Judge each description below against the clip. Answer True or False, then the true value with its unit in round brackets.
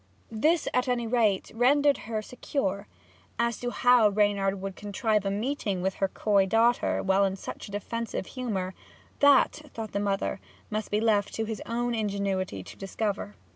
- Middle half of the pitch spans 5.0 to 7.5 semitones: False (3.2 semitones)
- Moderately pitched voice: False (215 Hz)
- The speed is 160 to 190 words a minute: True (170 wpm)